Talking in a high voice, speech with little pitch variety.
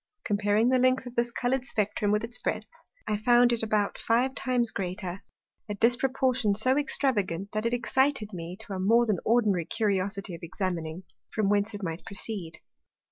No: high, 215 Hz; average, 3.6 semitones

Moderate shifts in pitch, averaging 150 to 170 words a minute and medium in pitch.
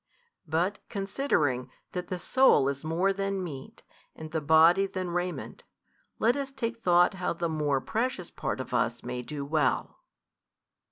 Yes: average, 5.0 semitones; average, 155 wpm; medium, 175 Hz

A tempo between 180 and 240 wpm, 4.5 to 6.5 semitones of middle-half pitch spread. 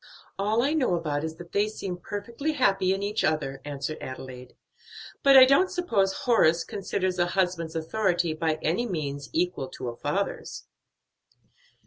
No: average, 160 wpm; average, 5.2 semitones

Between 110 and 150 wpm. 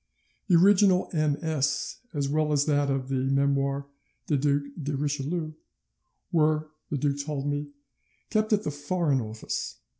Yes: average, 145 wpm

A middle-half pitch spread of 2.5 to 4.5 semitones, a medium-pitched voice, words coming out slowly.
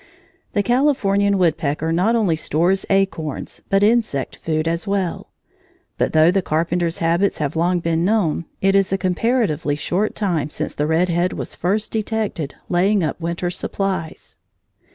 No: average, 3.4 semitones; medium, 180 Hz; average, 155 wpm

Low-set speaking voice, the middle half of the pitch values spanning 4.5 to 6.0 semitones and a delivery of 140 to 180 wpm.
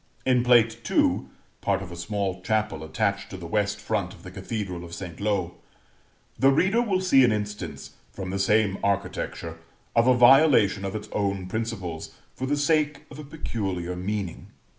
Yes: low, 105 Hz; average, 4.9 semitones; average, 175 wpm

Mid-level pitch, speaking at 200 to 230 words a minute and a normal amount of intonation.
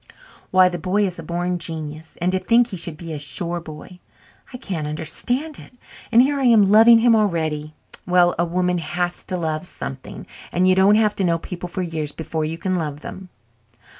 Yes: medium, 180 Hz; fast, 205 wpm; average, 3.4 semitones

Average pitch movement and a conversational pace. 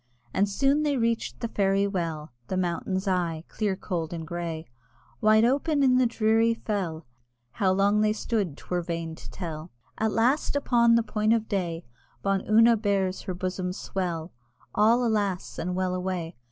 Yes: average, 4.3 semitones; average, 165 wpm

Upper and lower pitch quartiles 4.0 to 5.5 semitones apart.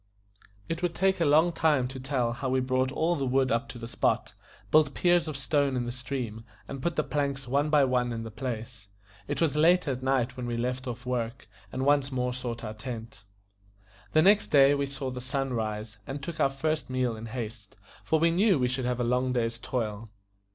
No: average, 3.1 semitones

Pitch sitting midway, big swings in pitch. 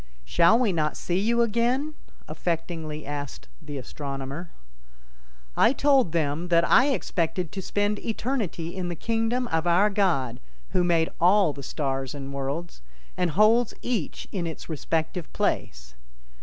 Yes: medium, 170 Hz; wide, 5.8 semitones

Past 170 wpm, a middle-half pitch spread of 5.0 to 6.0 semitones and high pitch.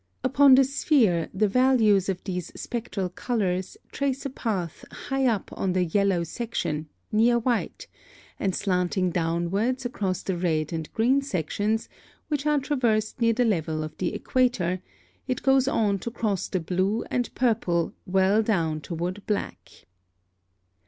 No: average, 145 wpm; wide, 5.4 semitones; high, 205 Hz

